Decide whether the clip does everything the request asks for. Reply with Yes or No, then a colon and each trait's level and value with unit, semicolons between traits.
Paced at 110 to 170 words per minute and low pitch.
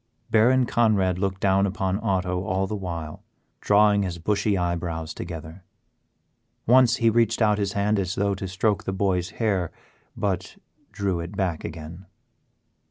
Yes: average, 150 wpm; very low, 95 Hz